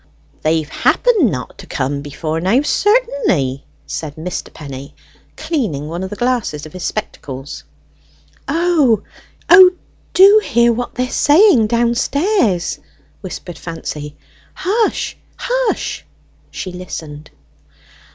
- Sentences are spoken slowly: Yes, slow, 110 wpm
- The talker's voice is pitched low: No, high, 205 Hz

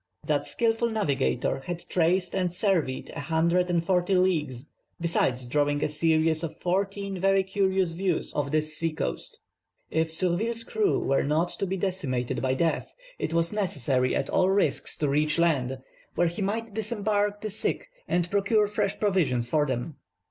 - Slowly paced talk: No, average, 165 wpm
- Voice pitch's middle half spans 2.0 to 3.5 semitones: No, average, 4.7 semitones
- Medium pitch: Yes, medium, 175 Hz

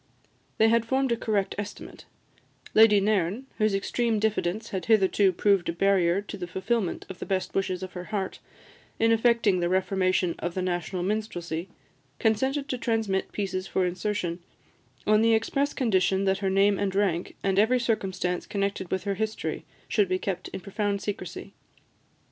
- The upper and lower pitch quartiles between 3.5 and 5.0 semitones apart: No, average, 2.9 semitones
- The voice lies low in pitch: No, high, 200 Hz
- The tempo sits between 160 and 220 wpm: Yes, average, 165 wpm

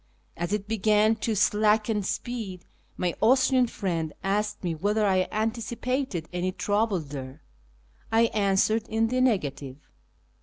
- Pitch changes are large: No, average, 3.5 semitones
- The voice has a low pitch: No, high, 210 Hz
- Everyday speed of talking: No, slow, 125 wpm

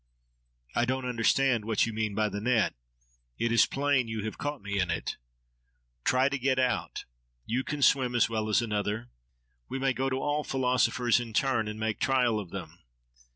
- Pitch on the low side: Yes, low, 120 Hz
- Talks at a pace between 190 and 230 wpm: Yes, average, 195 wpm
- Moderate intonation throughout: Yes, average, 3.4 semitones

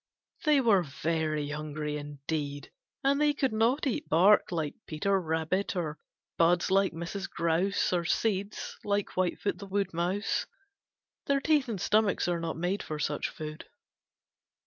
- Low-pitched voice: No, medium, 180 Hz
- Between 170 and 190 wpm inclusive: No, average, 145 wpm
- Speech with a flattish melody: No, average, 4.5 semitones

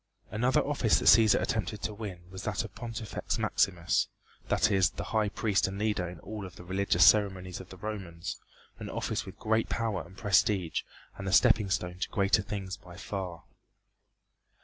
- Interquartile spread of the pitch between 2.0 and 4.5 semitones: Yes, average, 2.8 semitones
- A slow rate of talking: No, average, 180 wpm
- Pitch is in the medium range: No, low, 100 Hz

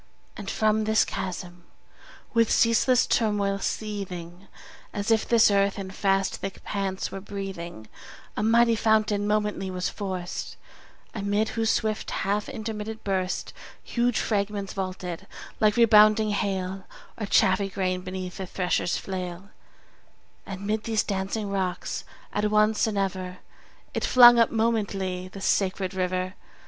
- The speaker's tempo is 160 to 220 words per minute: No, slow, 135 wpm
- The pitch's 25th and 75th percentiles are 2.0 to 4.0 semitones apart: Yes, narrow, 2.4 semitones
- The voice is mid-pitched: No, high, 200 Hz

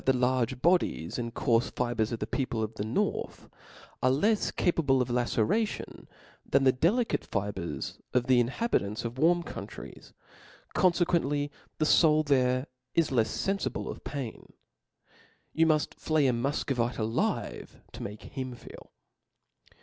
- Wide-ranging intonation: No, average, 4.9 semitones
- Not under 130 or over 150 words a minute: Yes, average, 145 wpm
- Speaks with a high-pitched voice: No, low, 130 Hz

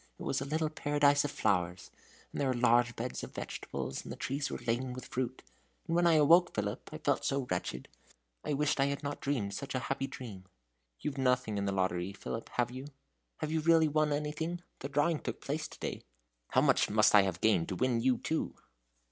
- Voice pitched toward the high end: No, low, 135 Hz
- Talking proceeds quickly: Yes, fast, 215 wpm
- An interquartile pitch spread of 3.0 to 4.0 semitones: No, average, 5.2 semitones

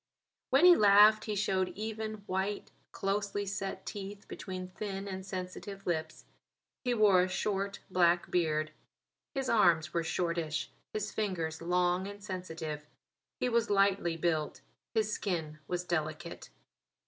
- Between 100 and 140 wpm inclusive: Yes, slow, 135 wpm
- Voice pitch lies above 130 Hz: Yes, high, 190 Hz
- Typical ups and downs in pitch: Yes, average, 3.2 semitones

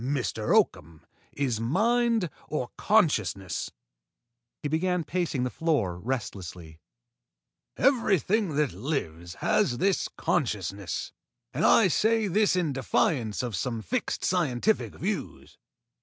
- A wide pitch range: Yes, wide, 8.8 semitones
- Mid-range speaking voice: Yes, medium, 145 Hz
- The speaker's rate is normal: No, slow, 110 wpm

